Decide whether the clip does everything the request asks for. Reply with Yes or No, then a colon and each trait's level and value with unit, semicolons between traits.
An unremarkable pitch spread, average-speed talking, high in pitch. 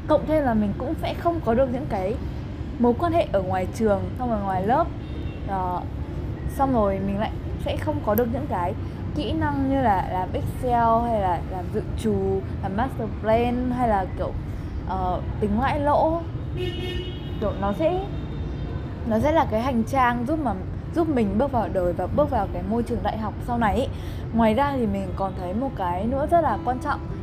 Yes: average, 3.8 semitones; average, 205 wpm; high, 240 Hz